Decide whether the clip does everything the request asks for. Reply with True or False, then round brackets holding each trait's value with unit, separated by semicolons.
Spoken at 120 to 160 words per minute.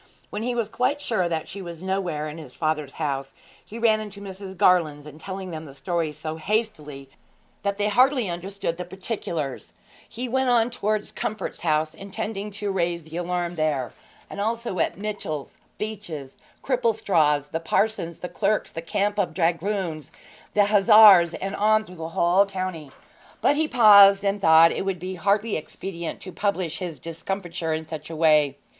False (175 wpm)